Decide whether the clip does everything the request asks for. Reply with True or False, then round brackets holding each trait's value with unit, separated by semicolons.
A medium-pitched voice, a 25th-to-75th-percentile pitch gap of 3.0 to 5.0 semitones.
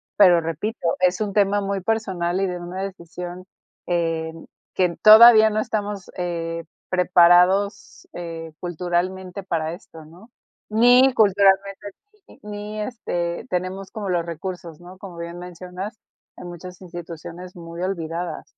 False (180 Hz; 2.6 semitones)